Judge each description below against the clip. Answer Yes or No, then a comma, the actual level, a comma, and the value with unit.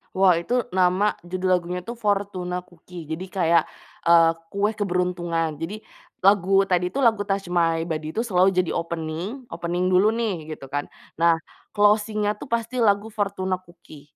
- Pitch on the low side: No, medium, 185 Hz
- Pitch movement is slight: No, average, 3.2 semitones